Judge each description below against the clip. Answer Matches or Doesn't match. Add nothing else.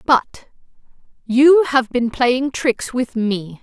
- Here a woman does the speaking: Matches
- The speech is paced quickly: Doesn't match